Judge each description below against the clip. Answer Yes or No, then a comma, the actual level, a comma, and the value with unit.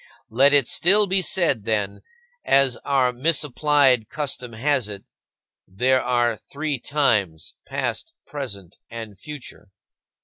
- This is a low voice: Yes, low, 130 Hz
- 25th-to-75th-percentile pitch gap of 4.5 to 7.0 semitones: Yes, average, 4.8 semitones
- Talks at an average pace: No, slow, 115 wpm